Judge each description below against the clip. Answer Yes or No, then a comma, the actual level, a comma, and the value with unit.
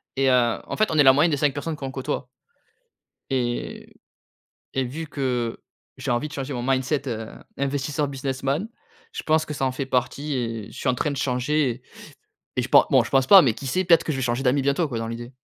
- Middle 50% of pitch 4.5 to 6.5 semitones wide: No, average, 2.7 semitones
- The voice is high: No, low, 135 Hz